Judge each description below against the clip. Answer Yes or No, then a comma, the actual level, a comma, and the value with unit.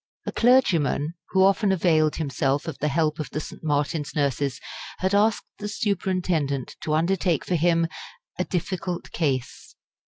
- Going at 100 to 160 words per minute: Yes, average, 150 wpm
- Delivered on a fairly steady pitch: No, average, 4.2 semitones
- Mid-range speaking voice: Yes, medium, 165 Hz